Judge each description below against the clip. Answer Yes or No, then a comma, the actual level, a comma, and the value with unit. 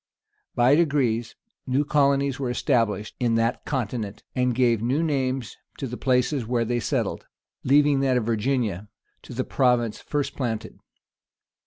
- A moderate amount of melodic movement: Yes, average, 3.0 semitones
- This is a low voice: Yes, low, 125 Hz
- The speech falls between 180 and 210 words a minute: No, average, 150 wpm